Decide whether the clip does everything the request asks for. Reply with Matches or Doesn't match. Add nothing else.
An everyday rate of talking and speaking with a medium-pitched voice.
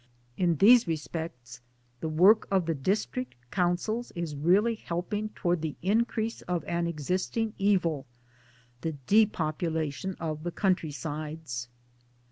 Doesn't match